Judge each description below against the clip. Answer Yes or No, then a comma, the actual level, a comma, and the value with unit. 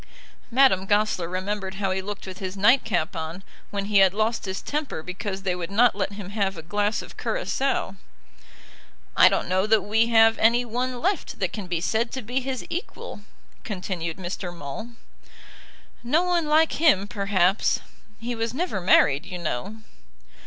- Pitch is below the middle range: No, high, 205 Hz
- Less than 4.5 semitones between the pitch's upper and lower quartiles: Yes, average, 4.0 semitones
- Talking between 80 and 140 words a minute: No, average, 170 wpm